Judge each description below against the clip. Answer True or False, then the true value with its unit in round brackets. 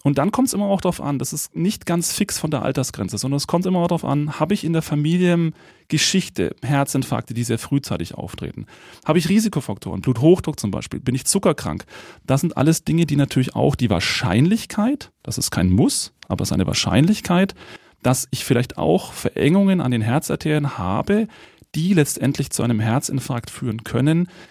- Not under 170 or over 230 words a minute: True (190 wpm)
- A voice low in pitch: False (150 Hz)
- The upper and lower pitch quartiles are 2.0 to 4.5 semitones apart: False (5.6 semitones)